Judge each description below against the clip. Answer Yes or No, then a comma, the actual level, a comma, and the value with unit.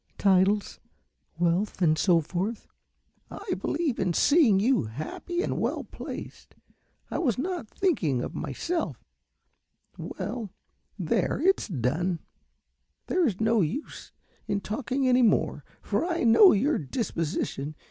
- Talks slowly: Yes, slow, 125 wpm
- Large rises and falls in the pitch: Yes, wide, 8.3 semitones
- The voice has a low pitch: No, high, 210 Hz